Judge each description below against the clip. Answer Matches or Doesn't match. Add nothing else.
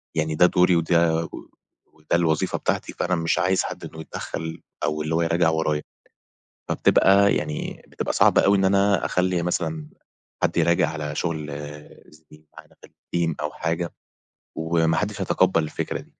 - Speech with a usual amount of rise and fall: Doesn't match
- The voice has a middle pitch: Doesn't match